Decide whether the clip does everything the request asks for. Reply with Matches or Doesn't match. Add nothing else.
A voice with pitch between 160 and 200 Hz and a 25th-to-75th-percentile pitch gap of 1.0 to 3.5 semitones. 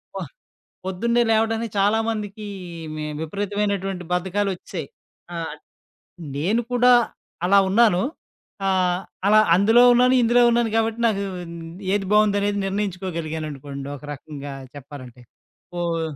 Doesn't match